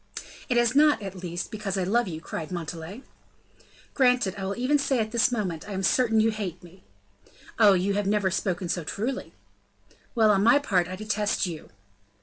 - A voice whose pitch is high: Yes, high, 200 Hz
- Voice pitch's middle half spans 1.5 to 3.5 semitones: No, average, 4.2 semitones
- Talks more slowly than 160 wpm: No, average, 195 wpm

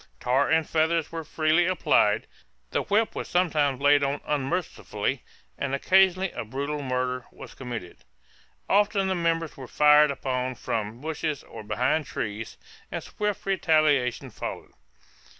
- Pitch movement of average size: Yes, average, 4.6 semitones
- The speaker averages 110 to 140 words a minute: Yes, slow, 135 wpm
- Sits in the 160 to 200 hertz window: No, medium, 150 Hz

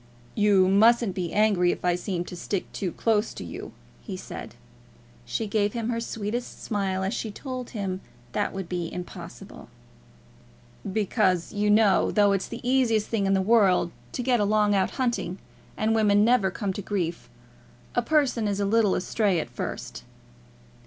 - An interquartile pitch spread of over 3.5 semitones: No, average, 3.0 semitones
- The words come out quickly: No, average, 175 wpm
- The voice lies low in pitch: No, high, 205 Hz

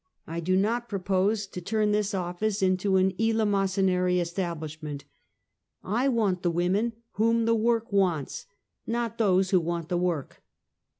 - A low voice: No, high, 190 Hz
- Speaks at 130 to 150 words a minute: Yes, average, 140 wpm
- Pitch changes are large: No, average, 3.5 semitones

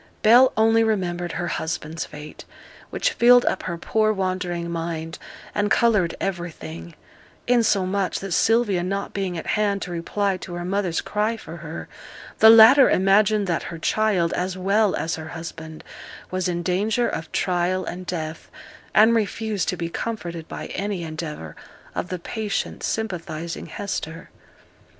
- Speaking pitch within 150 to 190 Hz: Yes, medium, 185 Hz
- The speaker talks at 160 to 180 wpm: No, average, 150 wpm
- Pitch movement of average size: Yes, average, 3.9 semitones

